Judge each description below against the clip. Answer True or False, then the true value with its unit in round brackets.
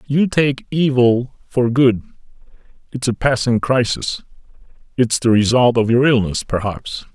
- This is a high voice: False (125 Hz)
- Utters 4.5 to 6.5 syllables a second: False (4.2 syllables/s)